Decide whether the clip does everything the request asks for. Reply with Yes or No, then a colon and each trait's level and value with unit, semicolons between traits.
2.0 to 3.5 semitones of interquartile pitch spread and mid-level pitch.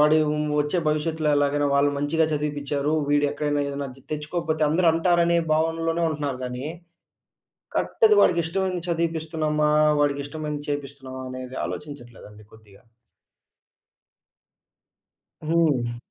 Yes: narrow, 2.4 semitones; medium, 150 Hz